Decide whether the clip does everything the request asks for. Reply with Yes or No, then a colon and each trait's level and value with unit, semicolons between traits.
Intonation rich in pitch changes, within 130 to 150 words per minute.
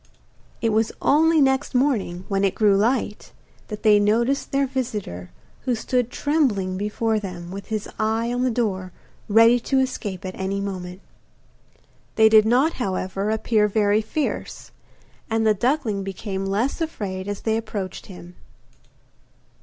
No: average, 3.8 semitones; average, 145 wpm